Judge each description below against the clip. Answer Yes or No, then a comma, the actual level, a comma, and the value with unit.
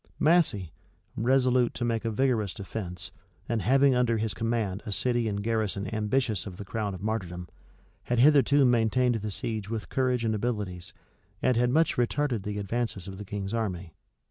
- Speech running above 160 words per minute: Yes, average, 170 wpm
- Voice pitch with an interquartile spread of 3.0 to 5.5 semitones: Yes, average, 3.4 semitones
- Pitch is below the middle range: Yes, low, 110 Hz